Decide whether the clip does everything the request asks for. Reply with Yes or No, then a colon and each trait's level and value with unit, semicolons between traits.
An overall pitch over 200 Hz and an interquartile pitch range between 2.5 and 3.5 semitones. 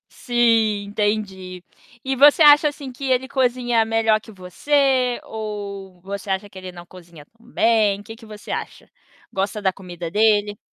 No: high, 215 Hz; average, 3.9 semitones